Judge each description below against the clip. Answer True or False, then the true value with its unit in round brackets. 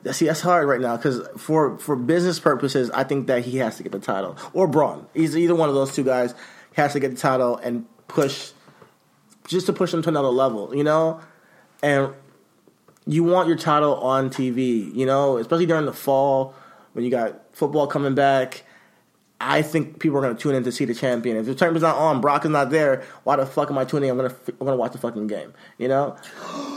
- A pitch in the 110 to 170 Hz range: True (140 Hz)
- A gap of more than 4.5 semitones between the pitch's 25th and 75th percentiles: False (3.4 semitones)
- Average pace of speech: False (235 wpm)